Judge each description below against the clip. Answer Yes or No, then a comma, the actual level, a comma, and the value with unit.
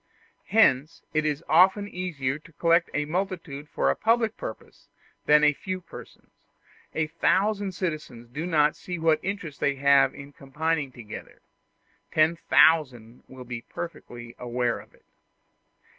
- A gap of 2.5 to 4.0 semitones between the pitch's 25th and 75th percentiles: No, average, 4.6 semitones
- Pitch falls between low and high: Yes, medium, 155 Hz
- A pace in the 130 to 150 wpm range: Yes, average, 145 wpm